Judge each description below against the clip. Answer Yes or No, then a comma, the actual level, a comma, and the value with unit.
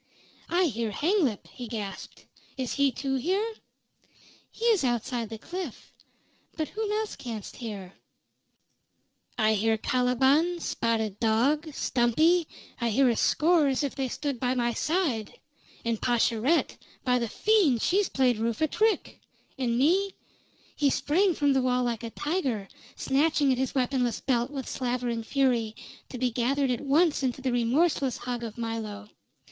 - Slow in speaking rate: No, average, 155 wpm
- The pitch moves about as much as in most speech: Yes, average, 4.6 semitones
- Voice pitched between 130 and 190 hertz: No, very high, 255 Hz